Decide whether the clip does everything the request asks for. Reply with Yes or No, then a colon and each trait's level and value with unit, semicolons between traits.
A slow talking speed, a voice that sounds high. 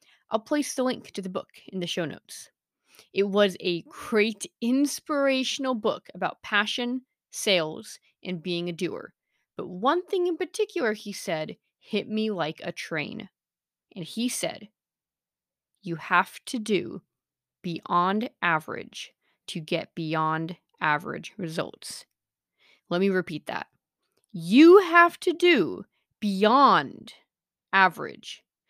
Yes: slow, 125 wpm; high, 205 Hz